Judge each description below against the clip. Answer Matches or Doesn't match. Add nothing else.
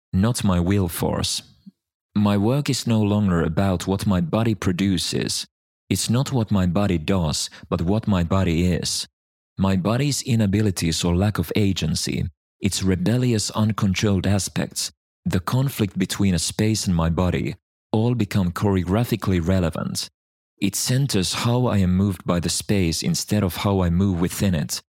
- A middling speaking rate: Matches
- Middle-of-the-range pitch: Doesn't match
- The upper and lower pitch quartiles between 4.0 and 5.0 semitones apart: Doesn't match